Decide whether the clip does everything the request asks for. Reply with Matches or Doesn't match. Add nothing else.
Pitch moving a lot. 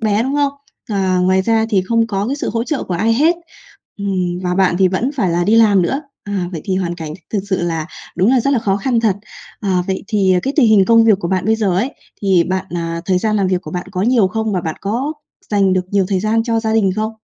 Doesn't match